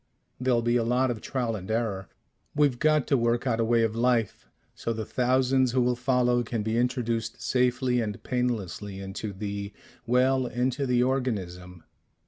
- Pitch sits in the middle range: No, low, 120 Hz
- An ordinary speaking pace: Yes, average, 170 wpm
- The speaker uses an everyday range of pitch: No, narrow, 2.3 semitones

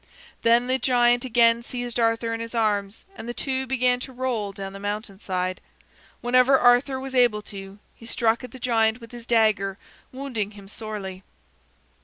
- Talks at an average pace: Yes, average, 175 wpm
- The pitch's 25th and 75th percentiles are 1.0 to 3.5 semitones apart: Yes, average, 3.0 semitones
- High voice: Yes, high, 230 Hz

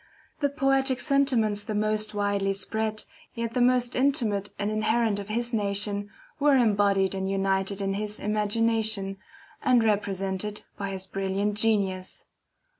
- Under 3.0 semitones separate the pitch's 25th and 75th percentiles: Yes, narrow, 2.6 semitones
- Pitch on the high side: Yes, high, 210 Hz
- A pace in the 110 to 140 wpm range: Yes, slow, 135 wpm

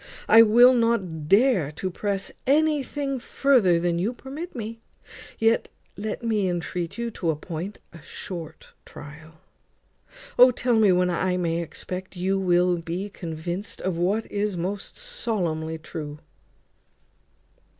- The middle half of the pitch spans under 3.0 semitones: No, average, 5.2 semitones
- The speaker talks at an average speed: No, slow, 130 wpm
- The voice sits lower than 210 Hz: Yes, high, 190 Hz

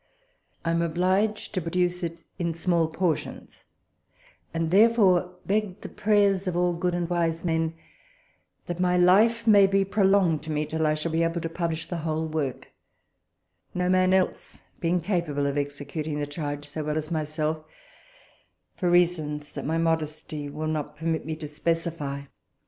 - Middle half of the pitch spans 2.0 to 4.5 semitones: Yes, average, 2.7 semitones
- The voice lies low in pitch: No, medium, 165 Hz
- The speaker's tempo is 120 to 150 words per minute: No, average, 165 wpm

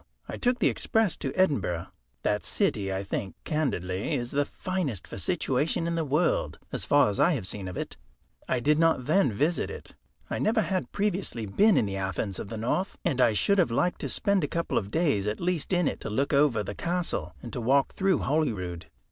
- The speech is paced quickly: Yes, fast, 215 wpm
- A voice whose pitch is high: No, medium, 140 Hz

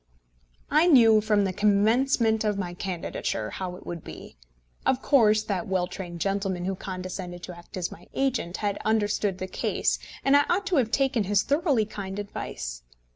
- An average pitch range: Yes, average, 3.7 semitones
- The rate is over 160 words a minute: Yes, average, 180 wpm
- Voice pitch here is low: No, high, 205 Hz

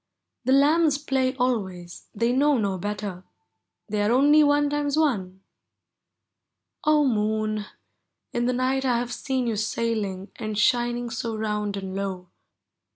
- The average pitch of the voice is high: Yes, high, 235 Hz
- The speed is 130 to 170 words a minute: Yes, average, 145 wpm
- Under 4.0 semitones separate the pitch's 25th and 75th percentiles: No, average, 4.4 semitones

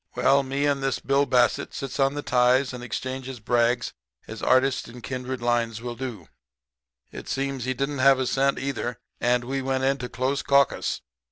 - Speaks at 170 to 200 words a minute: Yes, average, 180 wpm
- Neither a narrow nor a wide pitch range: No, narrow, 1.9 semitones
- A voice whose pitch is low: Yes, low, 130 Hz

